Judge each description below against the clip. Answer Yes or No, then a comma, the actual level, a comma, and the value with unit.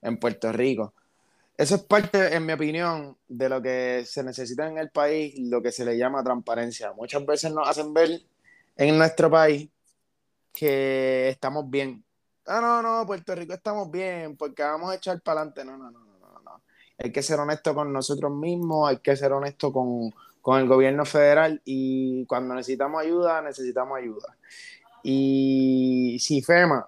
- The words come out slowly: No, average, 175 wpm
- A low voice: No, medium, 145 Hz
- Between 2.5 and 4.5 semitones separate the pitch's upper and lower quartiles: Yes, average, 3.4 semitones